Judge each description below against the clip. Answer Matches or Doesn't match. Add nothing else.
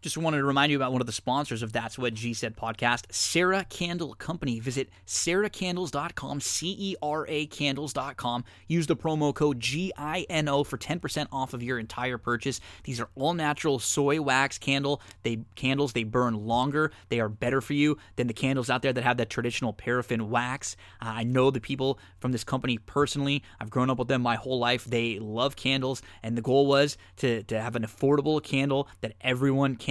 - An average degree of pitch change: Matches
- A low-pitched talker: Matches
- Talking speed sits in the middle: Matches